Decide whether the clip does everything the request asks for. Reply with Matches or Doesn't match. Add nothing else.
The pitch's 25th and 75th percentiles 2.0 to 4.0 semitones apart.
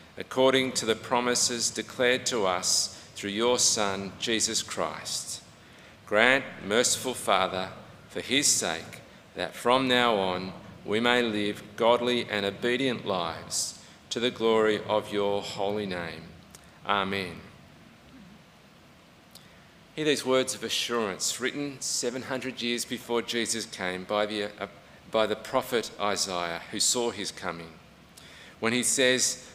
Matches